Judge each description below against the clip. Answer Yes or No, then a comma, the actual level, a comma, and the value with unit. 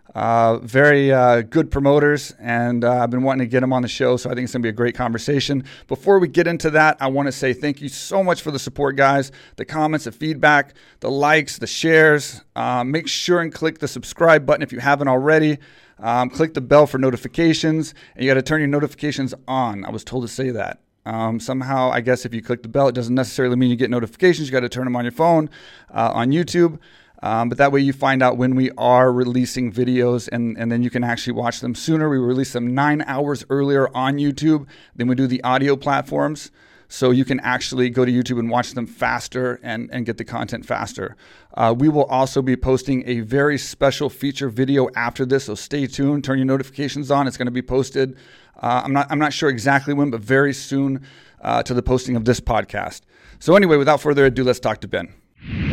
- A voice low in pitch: Yes, low, 130 Hz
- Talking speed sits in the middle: No, fast, 225 wpm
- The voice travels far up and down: No, narrow, 2.5 semitones